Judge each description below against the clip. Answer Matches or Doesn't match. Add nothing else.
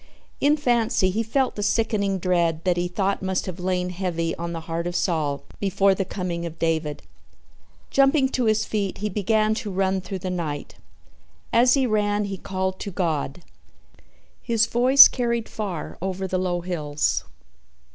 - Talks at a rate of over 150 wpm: Matches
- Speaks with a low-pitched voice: Doesn't match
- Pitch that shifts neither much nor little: Matches